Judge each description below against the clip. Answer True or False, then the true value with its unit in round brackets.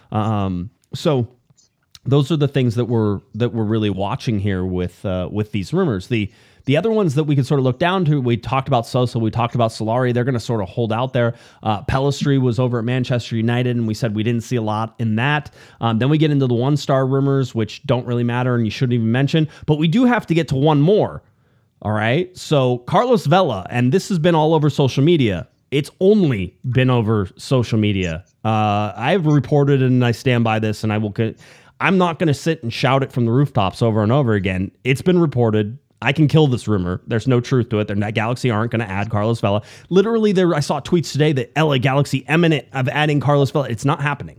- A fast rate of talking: True (235 wpm)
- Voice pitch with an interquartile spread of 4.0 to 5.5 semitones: True (4.5 semitones)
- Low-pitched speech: True (125 Hz)